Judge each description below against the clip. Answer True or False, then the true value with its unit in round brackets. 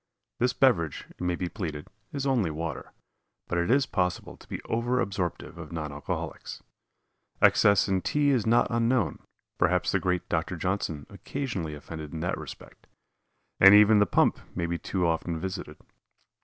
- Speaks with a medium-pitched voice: False (90 Hz)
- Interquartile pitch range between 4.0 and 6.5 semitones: True (5.6 semitones)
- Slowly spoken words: False (165 wpm)